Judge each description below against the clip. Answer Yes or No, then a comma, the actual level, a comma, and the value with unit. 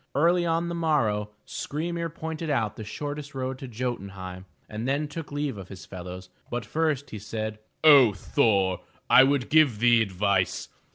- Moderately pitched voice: No, low, 125 Hz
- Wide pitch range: Yes, wide, 6.3 semitones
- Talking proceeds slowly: No, average, 170 wpm